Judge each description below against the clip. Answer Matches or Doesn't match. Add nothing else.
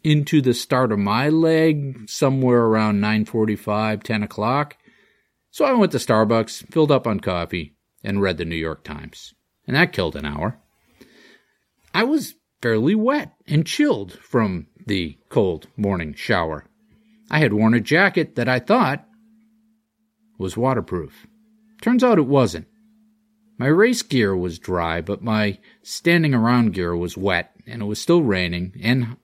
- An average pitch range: Doesn't match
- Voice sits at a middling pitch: Doesn't match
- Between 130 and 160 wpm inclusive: Matches